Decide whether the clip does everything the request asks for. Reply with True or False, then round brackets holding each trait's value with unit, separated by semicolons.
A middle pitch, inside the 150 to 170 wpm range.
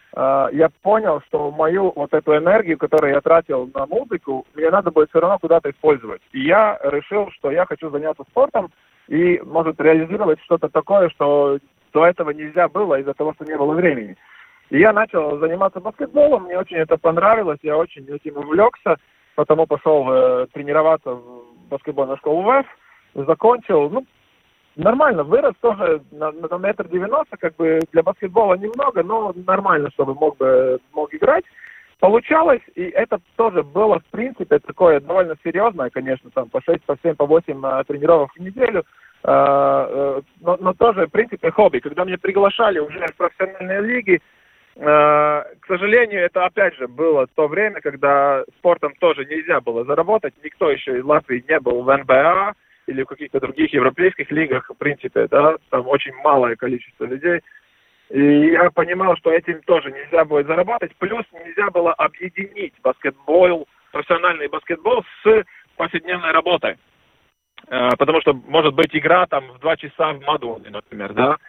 True (165 Hz; 160 wpm)